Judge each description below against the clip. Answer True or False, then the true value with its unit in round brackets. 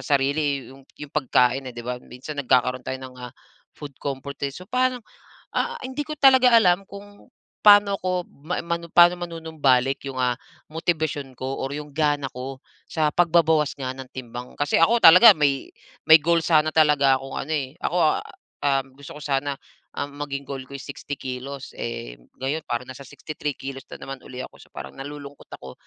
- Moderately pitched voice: True (145 Hz)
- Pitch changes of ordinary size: True (3.6 semitones)